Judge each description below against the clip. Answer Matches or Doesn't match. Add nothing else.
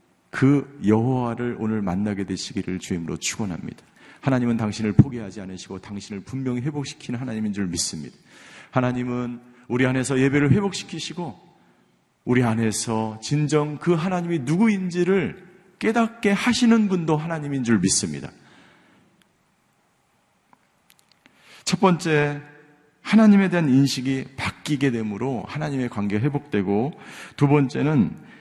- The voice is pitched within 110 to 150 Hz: Matches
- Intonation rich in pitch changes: Matches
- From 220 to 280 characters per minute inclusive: Doesn't match